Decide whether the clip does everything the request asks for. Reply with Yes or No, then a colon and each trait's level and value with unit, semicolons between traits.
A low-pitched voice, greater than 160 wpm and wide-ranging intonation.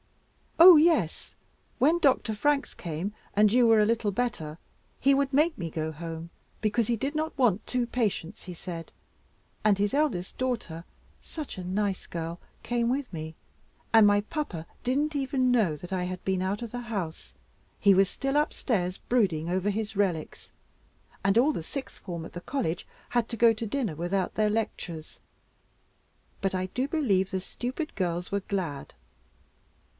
No: high, 210 Hz; average, 170 wpm; wide, 5.9 semitones